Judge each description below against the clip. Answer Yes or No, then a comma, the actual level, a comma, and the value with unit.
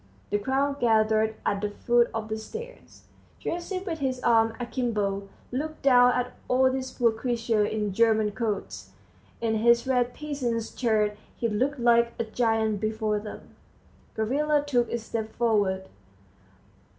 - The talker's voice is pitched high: Yes, high, 235 Hz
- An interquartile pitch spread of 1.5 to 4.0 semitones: Yes, average, 2.9 semitones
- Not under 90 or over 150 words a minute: Yes, average, 145 wpm